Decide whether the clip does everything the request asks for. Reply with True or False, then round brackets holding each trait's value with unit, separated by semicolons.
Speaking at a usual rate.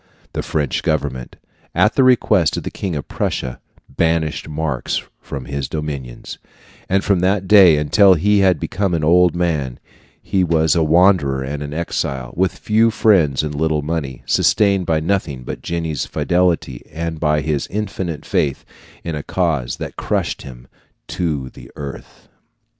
True (160 wpm)